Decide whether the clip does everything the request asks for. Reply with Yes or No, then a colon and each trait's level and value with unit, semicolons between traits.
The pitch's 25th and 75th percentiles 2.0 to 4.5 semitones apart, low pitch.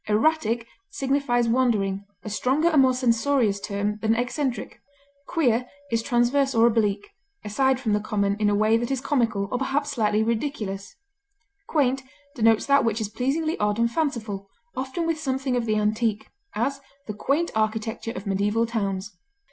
No: average, 4.1 semitones; high, 230 Hz